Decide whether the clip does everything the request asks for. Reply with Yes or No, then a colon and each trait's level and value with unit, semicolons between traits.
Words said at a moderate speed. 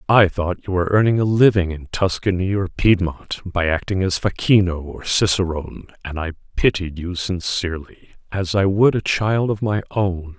Yes: average, 175 wpm